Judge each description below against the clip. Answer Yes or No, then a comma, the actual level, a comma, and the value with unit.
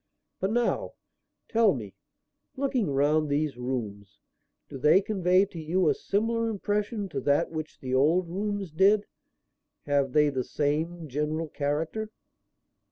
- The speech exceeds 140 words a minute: No, slow, 135 wpm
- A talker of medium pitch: Yes, medium, 160 Hz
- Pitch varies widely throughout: Yes, wide, 5.9 semitones